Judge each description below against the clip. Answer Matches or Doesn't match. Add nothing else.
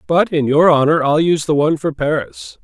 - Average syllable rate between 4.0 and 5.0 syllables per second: Doesn't match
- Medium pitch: Matches